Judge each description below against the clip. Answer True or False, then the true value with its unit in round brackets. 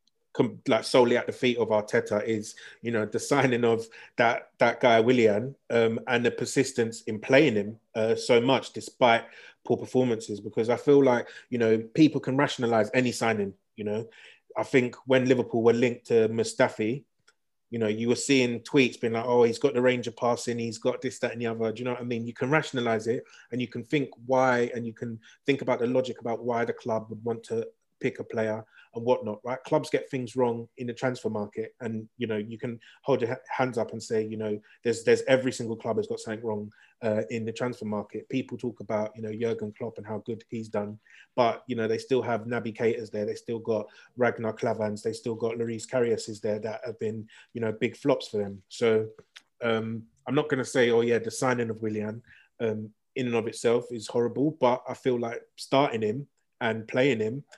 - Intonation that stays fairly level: True (2.2 semitones)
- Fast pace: True (220 wpm)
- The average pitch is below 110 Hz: False (115 Hz)